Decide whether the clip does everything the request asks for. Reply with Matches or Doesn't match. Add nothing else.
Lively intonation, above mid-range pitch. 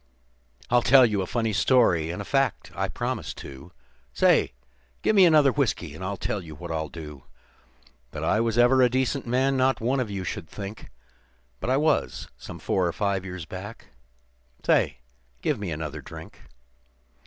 Doesn't match